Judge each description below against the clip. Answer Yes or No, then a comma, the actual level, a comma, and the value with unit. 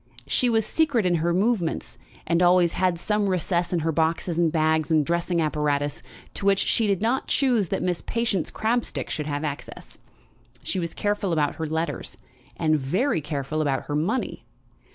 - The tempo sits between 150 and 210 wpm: Yes, average, 175 wpm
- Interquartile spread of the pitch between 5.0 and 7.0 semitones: No, average, 4.6 semitones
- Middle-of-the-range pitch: Yes, medium, 170 Hz